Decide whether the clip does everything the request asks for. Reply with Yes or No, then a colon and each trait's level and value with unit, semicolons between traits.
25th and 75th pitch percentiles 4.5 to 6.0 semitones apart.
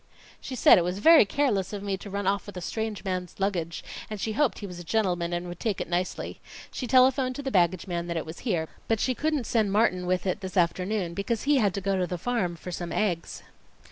No: average, 3.9 semitones